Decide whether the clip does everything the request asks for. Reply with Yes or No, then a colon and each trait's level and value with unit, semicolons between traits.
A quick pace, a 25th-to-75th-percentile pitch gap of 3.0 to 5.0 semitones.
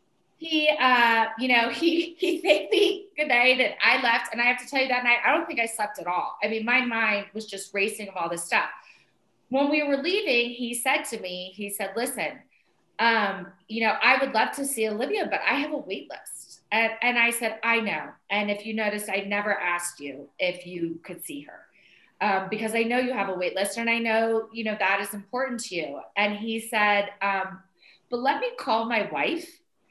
Yes: fast, 225 wpm; average, 4.0 semitones